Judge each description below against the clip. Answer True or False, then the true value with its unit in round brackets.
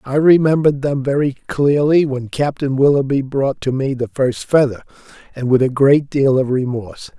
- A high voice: False (135 Hz)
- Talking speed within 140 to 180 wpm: True (175 wpm)